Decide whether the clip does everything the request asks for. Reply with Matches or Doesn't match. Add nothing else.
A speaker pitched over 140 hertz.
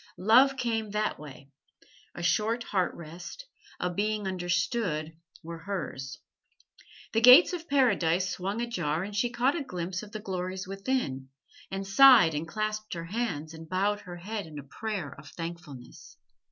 Matches